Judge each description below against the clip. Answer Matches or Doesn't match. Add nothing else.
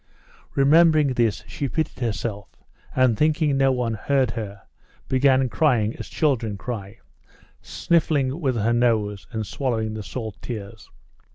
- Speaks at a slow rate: Matches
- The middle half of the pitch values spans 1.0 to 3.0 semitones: Doesn't match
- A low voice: Matches